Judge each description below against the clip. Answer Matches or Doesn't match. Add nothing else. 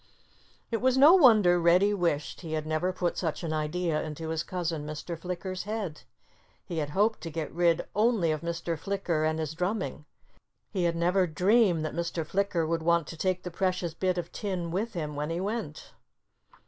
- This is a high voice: Doesn't match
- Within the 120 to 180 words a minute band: Doesn't match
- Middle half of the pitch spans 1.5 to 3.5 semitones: Matches